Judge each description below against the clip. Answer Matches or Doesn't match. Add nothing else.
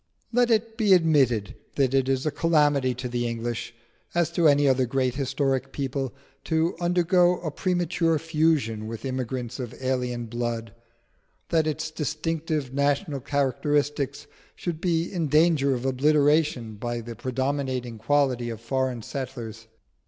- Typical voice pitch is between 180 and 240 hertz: Doesn't match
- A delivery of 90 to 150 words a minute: Matches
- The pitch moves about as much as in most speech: Matches